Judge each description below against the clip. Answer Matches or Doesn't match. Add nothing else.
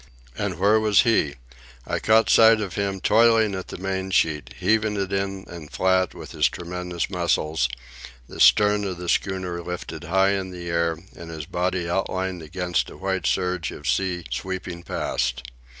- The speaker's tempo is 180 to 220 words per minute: Doesn't match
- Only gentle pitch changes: Matches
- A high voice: Doesn't match